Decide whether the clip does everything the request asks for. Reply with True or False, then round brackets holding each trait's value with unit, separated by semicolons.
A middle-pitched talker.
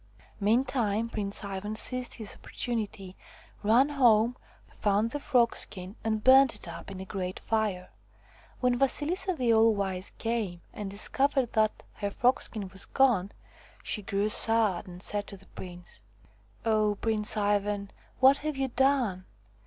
False (215 Hz)